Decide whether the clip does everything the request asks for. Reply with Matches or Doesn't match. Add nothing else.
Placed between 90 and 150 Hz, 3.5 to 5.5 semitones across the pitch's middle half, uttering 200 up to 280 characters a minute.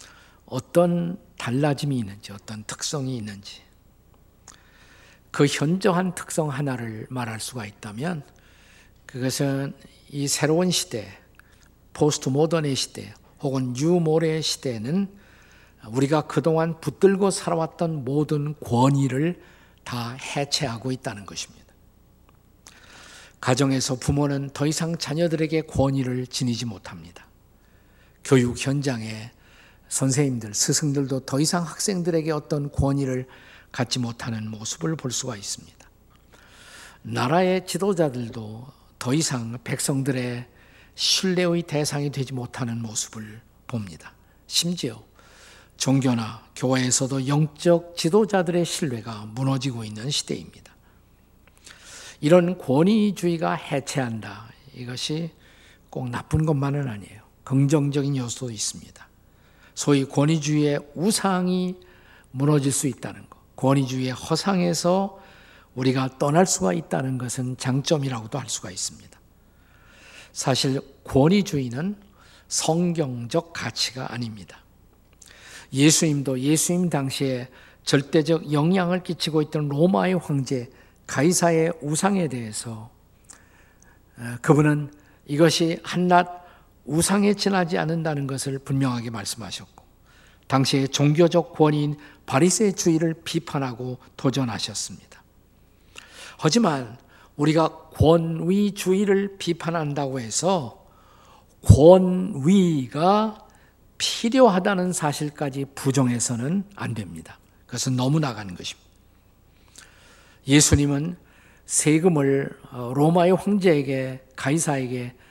Matches